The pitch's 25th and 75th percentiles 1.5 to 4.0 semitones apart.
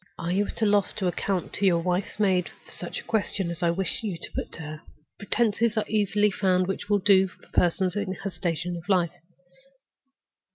Yes: narrow, 2.6 semitones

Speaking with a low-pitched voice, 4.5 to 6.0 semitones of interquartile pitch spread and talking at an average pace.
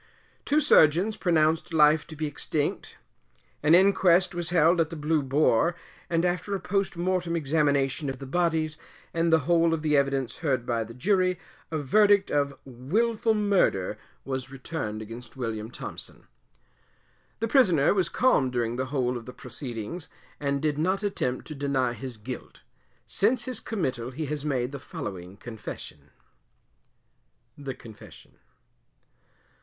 No: medium, 150 Hz; average, 5.3 semitones; average, 150 wpm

